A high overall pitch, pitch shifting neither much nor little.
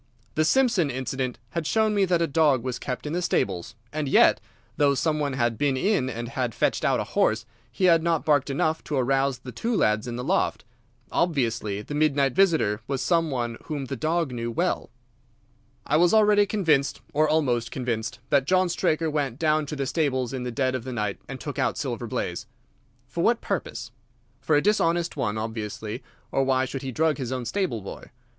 No: medium, 140 Hz; average, 4.6 semitones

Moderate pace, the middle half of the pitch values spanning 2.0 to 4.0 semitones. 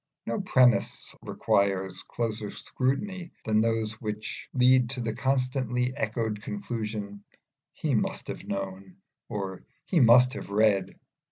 No: slow, 120 wpm; average, 3.3 semitones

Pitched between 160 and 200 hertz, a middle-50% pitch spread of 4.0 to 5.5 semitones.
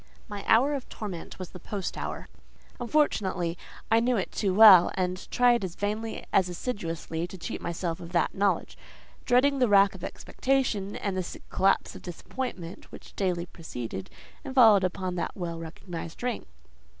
Yes: high, 190 Hz; average, 4.4 semitones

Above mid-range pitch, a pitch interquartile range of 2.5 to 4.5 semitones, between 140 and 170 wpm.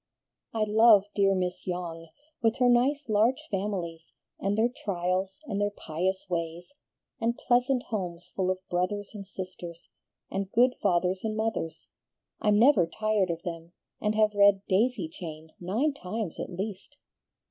Yes: high, 195 Hz; average, 3.6 semitones; average, 150 wpm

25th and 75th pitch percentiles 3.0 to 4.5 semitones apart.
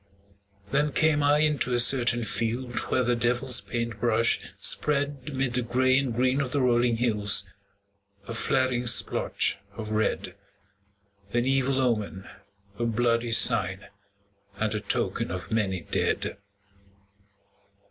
No: narrow, 2.5 semitones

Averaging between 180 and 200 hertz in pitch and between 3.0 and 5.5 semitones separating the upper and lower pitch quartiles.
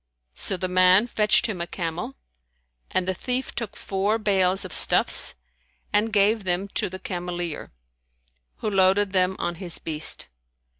No: high, 190 Hz; narrow, 2.5 semitones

